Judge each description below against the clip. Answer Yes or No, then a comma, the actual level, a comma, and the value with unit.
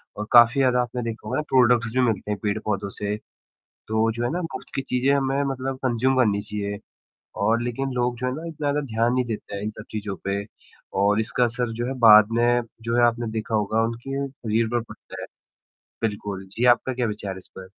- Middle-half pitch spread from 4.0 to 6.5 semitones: No, average, 3.0 semitones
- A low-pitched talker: Yes, low, 115 Hz